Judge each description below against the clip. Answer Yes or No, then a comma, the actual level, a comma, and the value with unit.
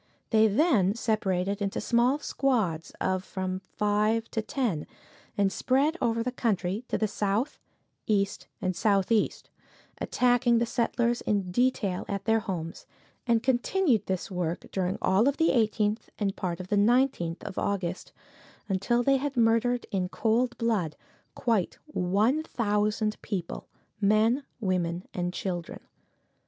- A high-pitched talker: Yes, high, 215 Hz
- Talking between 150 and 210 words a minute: No, average, 140 wpm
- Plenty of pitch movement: No, average, 4.1 semitones